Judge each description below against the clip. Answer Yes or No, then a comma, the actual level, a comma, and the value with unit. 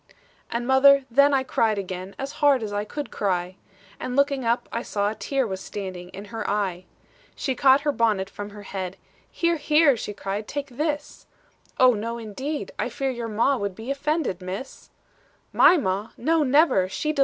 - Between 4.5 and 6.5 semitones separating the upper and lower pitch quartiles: Yes, wide, 5.4 semitones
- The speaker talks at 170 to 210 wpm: Yes, average, 175 wpm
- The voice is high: Yes, high, 230 Hz